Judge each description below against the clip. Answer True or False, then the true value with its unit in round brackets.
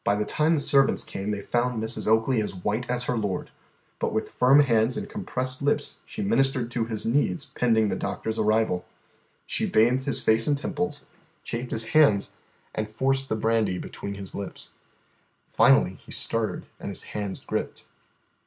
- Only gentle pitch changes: False (3.5 semitones)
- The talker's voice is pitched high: False (115 Hz)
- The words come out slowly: False (175 wpm)